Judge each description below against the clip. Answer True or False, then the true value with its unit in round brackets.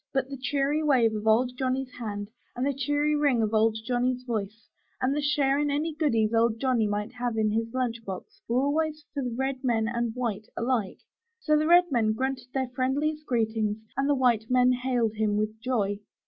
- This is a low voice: False (250 Hz)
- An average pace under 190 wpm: False (200 wpm)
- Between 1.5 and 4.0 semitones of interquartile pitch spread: True (3.7 semitones)